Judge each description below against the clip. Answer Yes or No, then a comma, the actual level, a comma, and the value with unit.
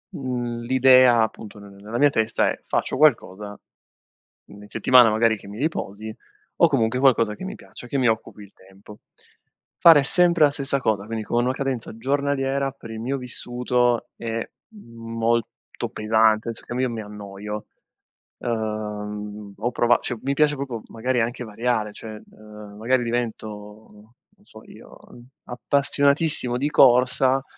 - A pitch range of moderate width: Yes, average, 3.3 semitones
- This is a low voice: Yes, low, 120 Hz